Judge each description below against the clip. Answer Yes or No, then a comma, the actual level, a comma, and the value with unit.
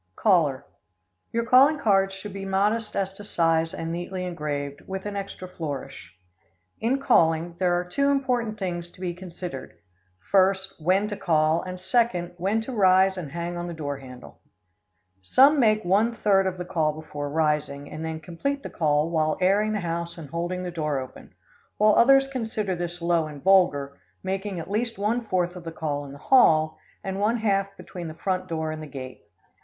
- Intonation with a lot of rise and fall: No, average, 4.2 semitones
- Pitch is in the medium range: Yes, medium, 180 Hz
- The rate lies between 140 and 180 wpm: No, average, 190 wpm